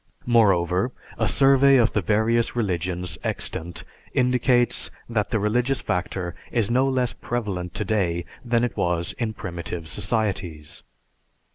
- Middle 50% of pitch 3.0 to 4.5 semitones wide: No, average, 5.2 semitones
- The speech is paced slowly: Yes, slow, 125 wpm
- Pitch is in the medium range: No, low, 110 Hz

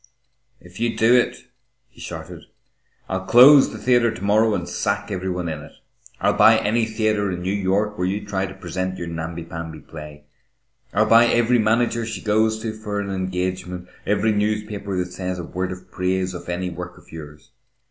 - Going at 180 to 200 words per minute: Yes, average, 190 wpm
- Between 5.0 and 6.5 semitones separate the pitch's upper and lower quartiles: No, average, 3.3 semitones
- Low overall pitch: Yes, very low, 95 Hz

